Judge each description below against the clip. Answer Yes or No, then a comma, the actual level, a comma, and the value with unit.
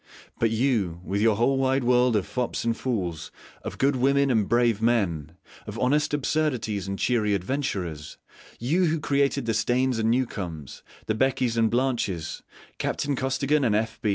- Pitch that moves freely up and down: No, average, 4.3 semitones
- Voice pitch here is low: Yes, low, 120 Hz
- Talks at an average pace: Yes, average, 160 wpm